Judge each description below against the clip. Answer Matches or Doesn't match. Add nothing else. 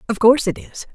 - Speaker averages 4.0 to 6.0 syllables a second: Doesn't match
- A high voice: Matches